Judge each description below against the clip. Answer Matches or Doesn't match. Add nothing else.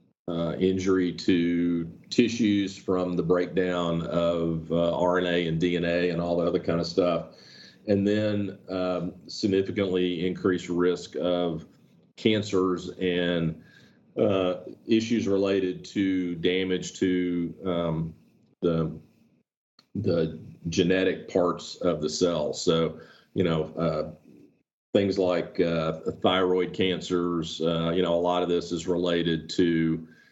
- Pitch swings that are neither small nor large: Doesn't match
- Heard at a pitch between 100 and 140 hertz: Doesn't match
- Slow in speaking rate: Matches